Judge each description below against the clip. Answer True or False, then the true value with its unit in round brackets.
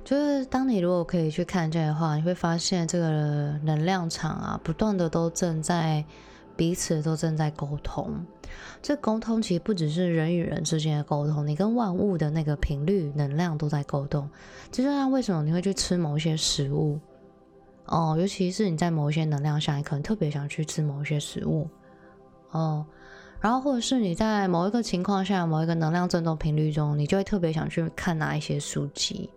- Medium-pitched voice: True (165 Hz)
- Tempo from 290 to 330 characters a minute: True (295 characters per minute)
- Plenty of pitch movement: False (3.7 semitones)